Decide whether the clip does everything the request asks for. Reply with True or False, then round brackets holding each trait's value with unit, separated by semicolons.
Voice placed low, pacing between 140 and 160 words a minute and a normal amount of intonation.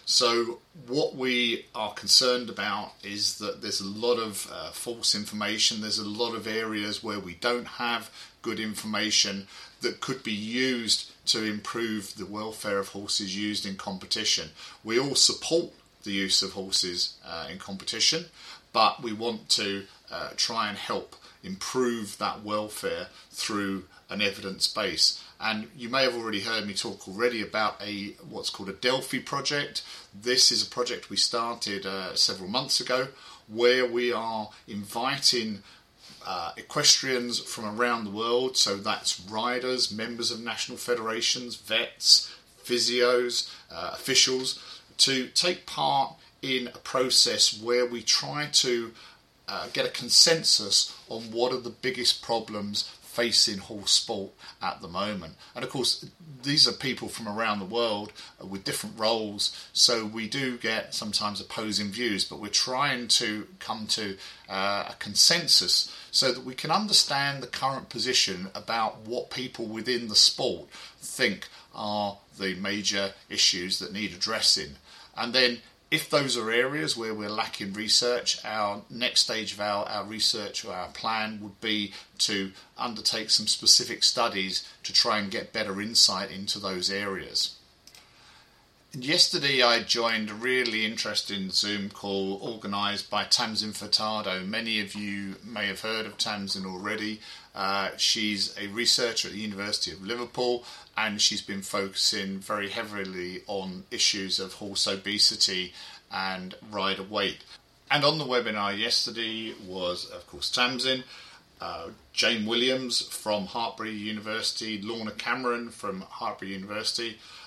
True (110 Hz; 150 wpm; 3.1 semitones)